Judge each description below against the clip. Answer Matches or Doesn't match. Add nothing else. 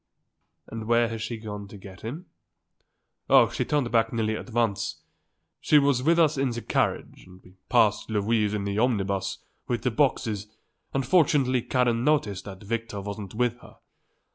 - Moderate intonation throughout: Matches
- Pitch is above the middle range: Doesn't match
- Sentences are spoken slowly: Doesn't match